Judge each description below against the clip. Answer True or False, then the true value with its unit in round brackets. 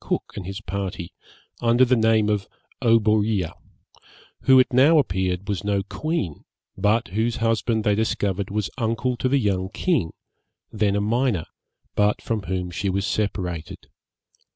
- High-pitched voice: False (105 Hz)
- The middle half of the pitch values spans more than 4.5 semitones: False (3.1 semitones)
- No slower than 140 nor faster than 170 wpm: True (150 wpm)